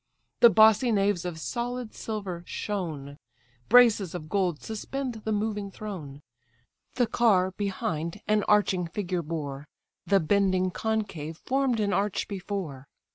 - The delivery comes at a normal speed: No, slow, 130 wpm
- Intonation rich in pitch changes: No, average, 4.1 semitones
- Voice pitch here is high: Yes, high, 200 Hz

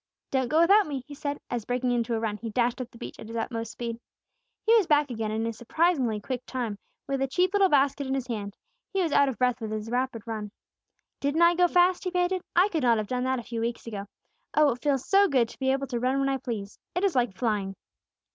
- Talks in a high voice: Yes, very high, 255 Hz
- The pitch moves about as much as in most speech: Yes, average, 4.4 semitones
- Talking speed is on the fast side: Yes, fast, 260 wpm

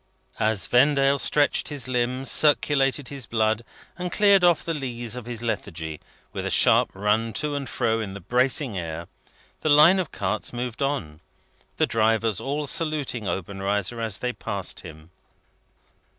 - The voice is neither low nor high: No, low, 120 Hz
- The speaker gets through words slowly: No, average, 155 wpm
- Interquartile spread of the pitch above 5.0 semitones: Yes, wide, 5.5 semitones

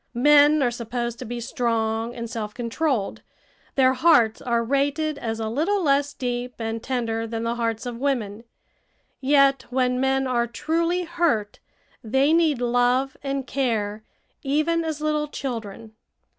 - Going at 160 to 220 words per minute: No, average, 145 wpm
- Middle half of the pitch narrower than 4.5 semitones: Yes, average, 3.8 semitones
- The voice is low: No, very high, 250 Hz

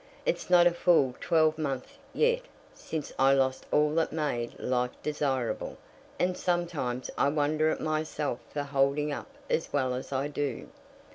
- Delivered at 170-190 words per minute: No, average, 150 wpm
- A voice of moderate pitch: Yes, medium, 150 Hz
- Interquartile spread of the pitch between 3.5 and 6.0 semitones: No, average, 2.9 semitones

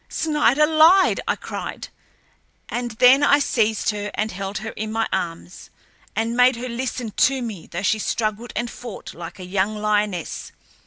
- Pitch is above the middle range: Yes, high, 220 Hz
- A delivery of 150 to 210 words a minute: Yes, average, 165 wpm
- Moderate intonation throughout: Yes, average, 3.3 semitones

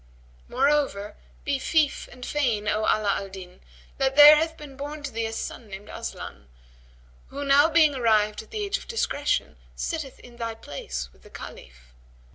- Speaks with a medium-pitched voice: No, very high, 250 Hz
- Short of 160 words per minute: No, average, 170 wpm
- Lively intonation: Yes, wide, 6.0 semitones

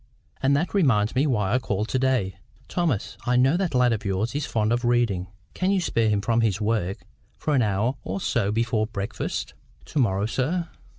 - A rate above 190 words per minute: Yes, average, 200 wpm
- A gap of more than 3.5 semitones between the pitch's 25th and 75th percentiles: Yes, average, 4.2 semitones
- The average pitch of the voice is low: Yes, low, 115 Hz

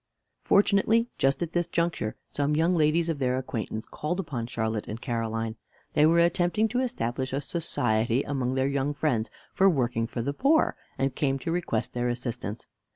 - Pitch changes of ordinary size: No, wide, 6.0 semitones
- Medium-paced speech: Yes, average, 175 wpm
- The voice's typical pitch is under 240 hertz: Yes, medium, 140 Hz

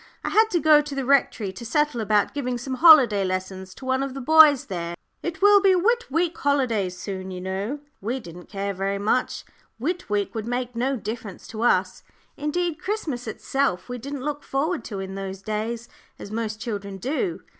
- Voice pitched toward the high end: Yes, high, 245 Hz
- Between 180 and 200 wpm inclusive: Yes, average, 195 wpm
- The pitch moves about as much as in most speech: No, wide, 6.7 semitones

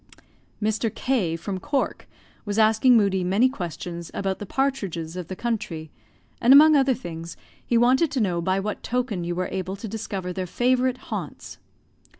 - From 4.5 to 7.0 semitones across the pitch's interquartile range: Yes, wide, 5.5 semitones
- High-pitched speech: Yes, high, 205 Hz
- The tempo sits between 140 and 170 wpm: Yes, average, 165 wpm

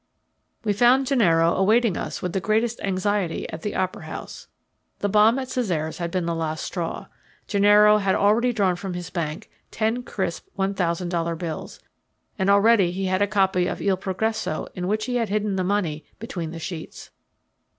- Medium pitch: No, high, 195 Hz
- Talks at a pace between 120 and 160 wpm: No, average, 180 wpm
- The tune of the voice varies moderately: Yes, average, 3.5 semitones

